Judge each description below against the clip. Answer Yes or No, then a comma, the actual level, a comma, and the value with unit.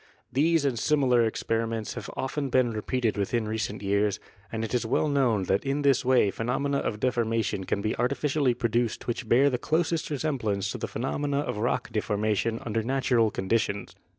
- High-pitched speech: No, low, 120 Hz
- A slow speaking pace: No, average, 180 wpm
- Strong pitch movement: No, average, 3.9 semitones